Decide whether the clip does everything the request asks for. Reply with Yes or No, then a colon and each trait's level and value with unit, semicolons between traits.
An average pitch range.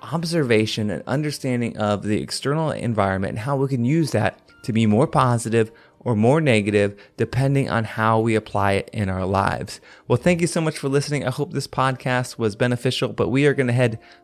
Yes: average, 4.3 semitones